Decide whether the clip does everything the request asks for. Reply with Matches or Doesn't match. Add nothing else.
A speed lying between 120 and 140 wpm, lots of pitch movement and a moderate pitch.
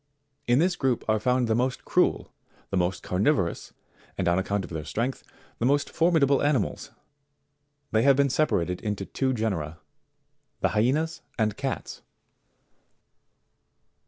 Doesn't match